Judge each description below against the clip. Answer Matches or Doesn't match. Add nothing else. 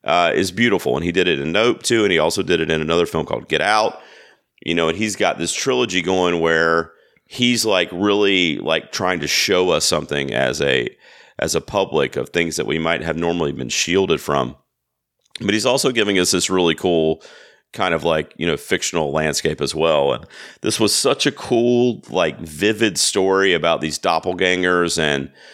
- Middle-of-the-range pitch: Doesn't match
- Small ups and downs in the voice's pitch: Doesn't match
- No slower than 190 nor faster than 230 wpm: Matches